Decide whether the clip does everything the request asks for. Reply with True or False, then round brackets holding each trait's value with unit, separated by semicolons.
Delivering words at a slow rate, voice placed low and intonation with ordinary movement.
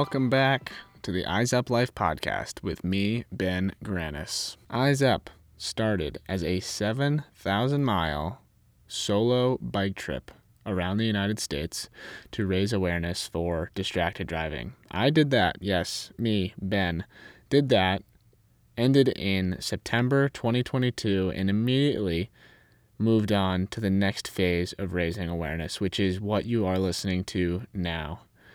True (130 wpm; 100 Hz; 4.4 semitones)